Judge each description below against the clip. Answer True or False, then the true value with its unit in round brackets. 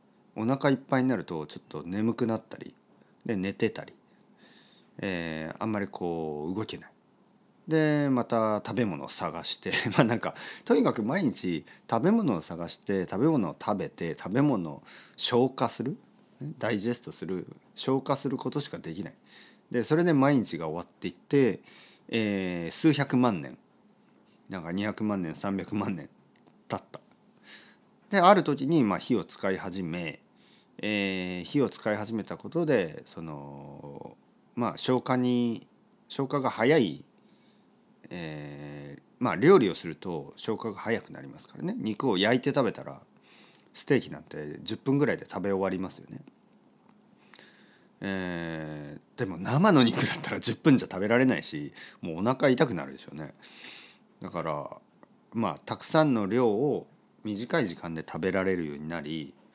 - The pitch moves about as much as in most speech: False (7.9 semitones)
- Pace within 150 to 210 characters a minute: False (275 characters per minute)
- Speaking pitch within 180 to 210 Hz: False (110 Hz)